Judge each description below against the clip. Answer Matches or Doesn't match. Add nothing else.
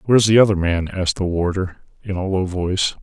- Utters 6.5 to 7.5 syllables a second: Doesn't match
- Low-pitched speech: Matches